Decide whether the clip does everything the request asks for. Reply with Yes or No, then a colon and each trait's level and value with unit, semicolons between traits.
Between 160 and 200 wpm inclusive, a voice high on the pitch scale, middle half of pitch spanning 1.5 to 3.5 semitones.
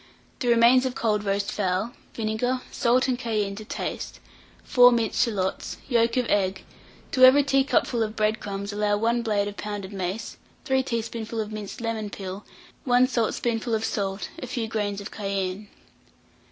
Yes: average, 165 wpm; high, 220 Hz; average, 2.8 semitones